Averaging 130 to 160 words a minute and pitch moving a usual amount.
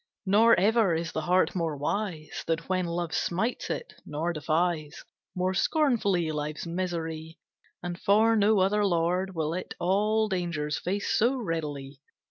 Yes: average, 145 wpm; average, 3.8 semitones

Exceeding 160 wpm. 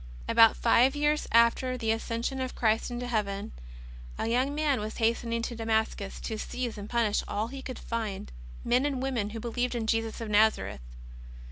Yes: average, 175 wpm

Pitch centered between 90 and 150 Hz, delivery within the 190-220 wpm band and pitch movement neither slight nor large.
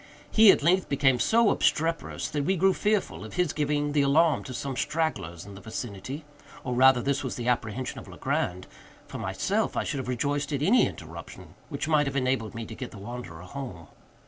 Yes: medium, 140 Hz; average, 195 wpm; average, 4.0 semitones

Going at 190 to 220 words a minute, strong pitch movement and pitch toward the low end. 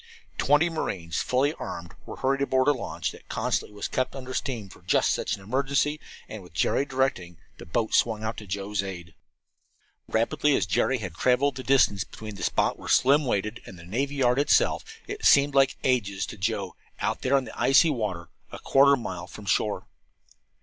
Yes: average, 200 wpm; wide, 5.7 semitones; low, 125 Hz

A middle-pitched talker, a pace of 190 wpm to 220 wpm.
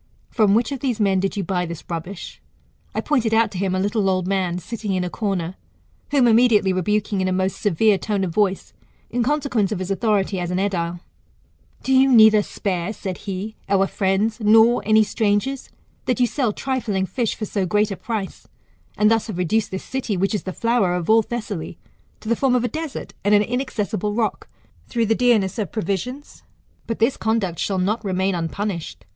No: high, 210 Hz; average, 200 wpm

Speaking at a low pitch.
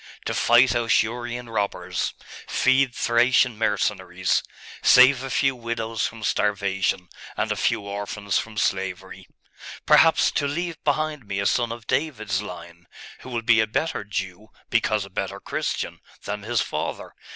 Yes: low, 115 Hz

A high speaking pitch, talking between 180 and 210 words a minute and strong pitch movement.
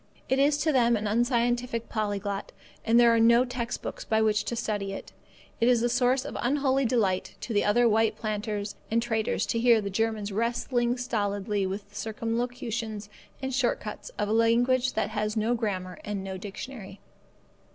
No: high, 225 Hz; average, 185 wpm; average, 2.7 semitones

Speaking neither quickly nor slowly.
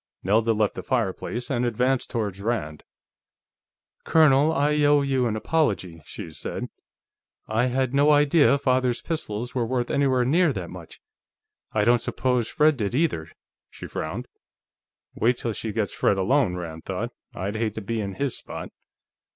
Yes: average, 160 wpm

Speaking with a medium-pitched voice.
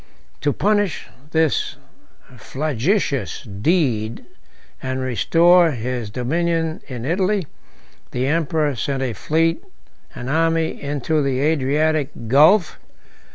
Yes: medium, 150 Hz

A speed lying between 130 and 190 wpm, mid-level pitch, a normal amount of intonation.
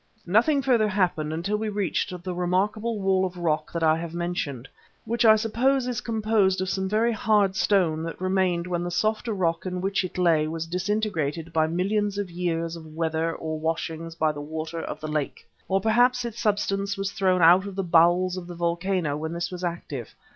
No: average, 200 wpm; medium, 180 Hz; average, 3.7 semitones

